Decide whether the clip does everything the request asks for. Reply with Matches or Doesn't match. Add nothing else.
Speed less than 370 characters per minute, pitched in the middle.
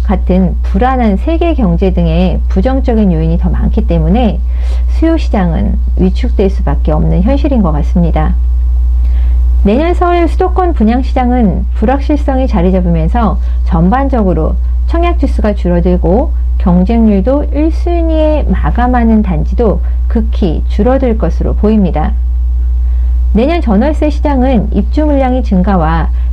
Matches